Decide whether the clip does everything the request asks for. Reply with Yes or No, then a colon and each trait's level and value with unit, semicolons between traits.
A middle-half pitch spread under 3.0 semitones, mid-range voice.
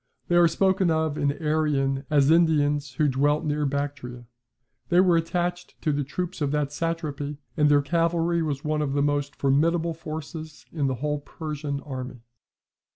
Yes: narrow, 2.6 semitones; medium, 150 Hz